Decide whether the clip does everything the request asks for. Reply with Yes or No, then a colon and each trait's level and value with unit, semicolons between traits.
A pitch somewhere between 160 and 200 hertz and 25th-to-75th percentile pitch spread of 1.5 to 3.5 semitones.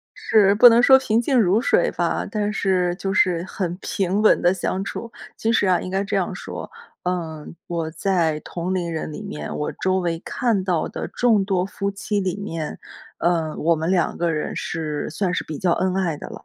Yes: medium, 185 Hz; average, 3.1 semitones